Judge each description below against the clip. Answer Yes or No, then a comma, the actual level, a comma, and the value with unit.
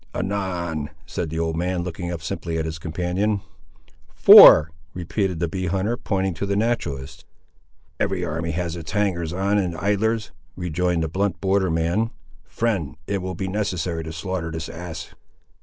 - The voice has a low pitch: Yes, very low, 90 Hz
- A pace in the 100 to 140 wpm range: No, average, 160 wpm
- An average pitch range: Yes, average, 3.1 semitones